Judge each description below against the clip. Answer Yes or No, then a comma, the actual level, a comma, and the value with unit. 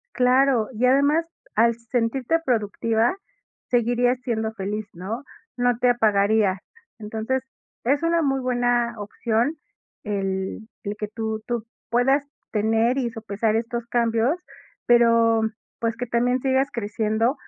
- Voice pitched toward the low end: No, high, 235 Hz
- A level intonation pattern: Yes, narrow, 2.3 semitones